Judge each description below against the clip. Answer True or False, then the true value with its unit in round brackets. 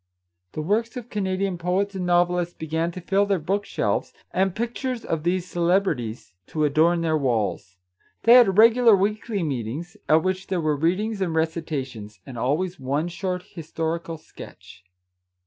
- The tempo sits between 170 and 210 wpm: False (160 wpm)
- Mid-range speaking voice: True (175 Hz)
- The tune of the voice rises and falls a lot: False (3.9 semitones)